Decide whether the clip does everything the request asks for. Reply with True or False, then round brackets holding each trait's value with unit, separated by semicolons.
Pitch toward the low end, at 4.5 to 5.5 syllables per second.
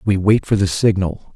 True (100 Hz; 5.0 syllables/s)